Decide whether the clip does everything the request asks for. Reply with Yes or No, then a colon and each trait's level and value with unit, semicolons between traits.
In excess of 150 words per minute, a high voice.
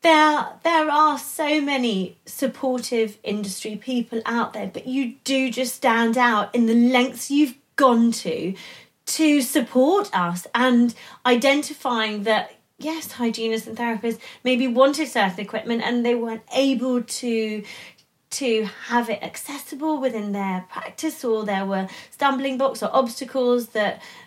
No: average, 140 wpm; high, 245 Hz